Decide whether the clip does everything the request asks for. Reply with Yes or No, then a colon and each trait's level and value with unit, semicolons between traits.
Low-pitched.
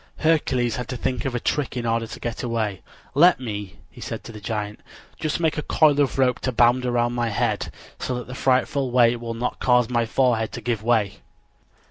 Yes: low, 120 Hz